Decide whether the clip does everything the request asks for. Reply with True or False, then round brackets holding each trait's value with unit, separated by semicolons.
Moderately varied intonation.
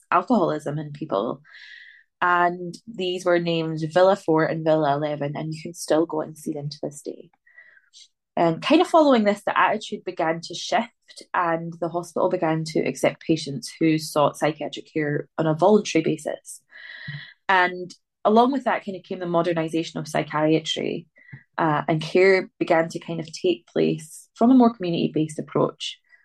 True (3.2 semitones)